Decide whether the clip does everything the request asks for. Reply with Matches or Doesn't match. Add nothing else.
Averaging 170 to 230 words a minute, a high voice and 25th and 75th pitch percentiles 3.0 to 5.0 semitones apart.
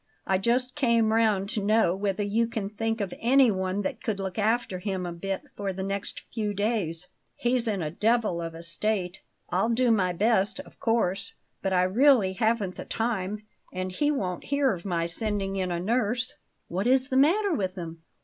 Matches